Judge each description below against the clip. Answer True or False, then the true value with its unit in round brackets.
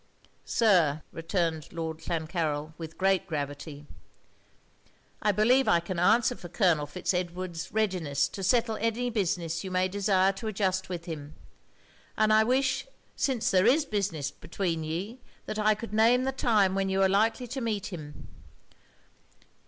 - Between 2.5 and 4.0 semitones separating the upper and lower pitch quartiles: False (4.7 semitones)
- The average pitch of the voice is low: False (190 Hz)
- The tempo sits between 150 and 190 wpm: True (155 wpm)